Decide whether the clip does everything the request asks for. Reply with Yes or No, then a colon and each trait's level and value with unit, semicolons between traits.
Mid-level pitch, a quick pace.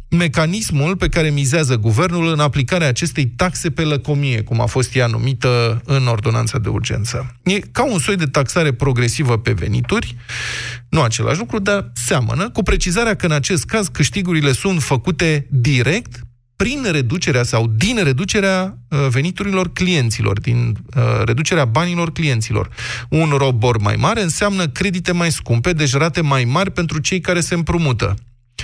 No: medium, 145 Hz; average, 150 wpm